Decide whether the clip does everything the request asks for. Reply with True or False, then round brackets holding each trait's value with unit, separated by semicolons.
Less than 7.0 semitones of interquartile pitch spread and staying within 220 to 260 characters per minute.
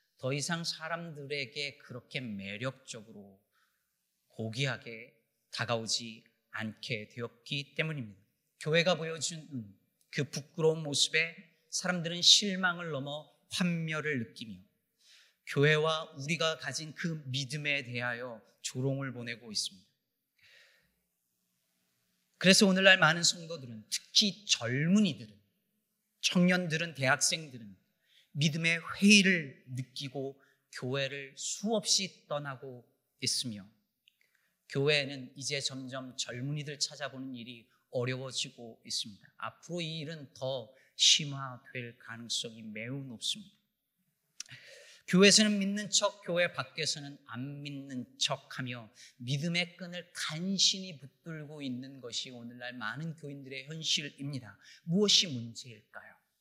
True (5.2 semitones; 255 characters per minute)